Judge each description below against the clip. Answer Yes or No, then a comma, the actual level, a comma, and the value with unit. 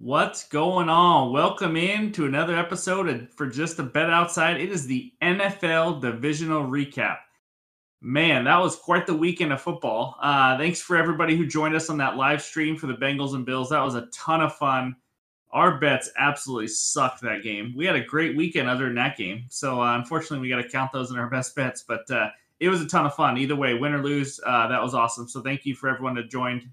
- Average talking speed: No, fast, 225 wpm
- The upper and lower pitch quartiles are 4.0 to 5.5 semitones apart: Yes, average, 4.3 semitones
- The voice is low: No, medium, 145 Hz